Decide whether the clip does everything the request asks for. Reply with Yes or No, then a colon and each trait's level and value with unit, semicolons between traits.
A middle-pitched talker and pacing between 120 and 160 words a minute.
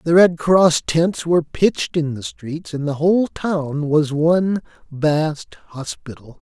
Yes: medium, 160 Hz; average, 155 wpm